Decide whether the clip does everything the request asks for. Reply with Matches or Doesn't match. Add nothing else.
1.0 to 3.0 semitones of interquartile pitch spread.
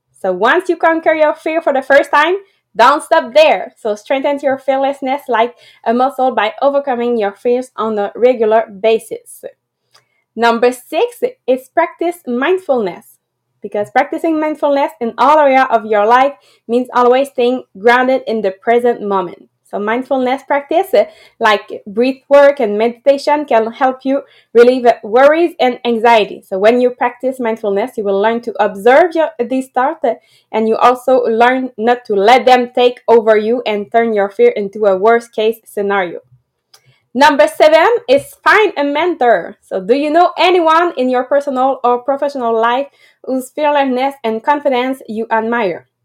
Doesn't match